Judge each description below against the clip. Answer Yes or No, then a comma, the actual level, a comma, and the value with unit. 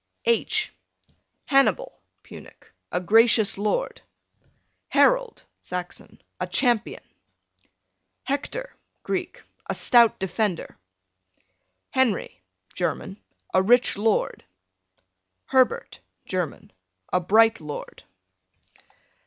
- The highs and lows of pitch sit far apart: Yes, wide, 5.8 semitones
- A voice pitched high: Yes, high, 225 Hz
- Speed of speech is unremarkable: No, slow, 80 wpm